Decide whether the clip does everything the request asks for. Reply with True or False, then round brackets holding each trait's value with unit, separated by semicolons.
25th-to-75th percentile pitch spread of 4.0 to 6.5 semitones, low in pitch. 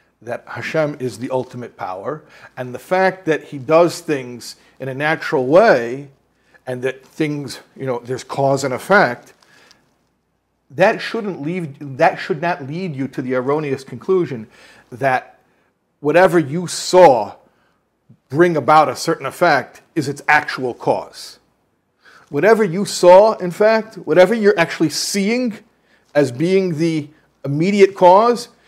False (5.3 semitones; 160 Hz)